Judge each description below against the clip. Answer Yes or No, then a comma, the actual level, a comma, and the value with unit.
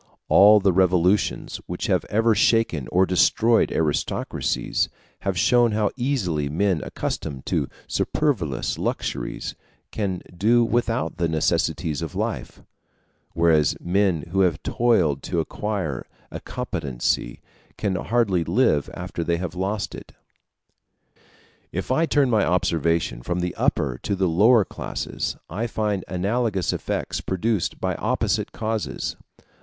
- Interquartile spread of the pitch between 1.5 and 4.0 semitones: No, average, 4.8 semitones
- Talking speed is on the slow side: Yes, slow, 130 wpm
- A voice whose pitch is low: Yes, very low, 95 Hz